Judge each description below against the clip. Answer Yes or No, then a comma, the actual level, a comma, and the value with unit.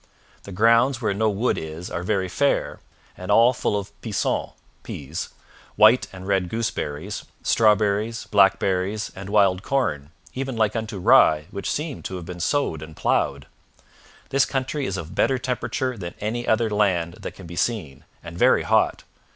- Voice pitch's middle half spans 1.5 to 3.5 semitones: No, average, 4.3 semitones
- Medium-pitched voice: No, low, 105 Hz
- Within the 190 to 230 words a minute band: No, average, 165 wpm